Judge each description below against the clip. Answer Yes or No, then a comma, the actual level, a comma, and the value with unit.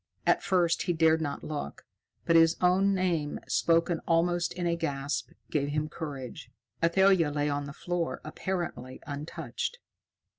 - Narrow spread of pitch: No, average, 3.2 semitones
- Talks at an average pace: Yes, average, 145 wpm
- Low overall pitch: No, medium, 165 Hz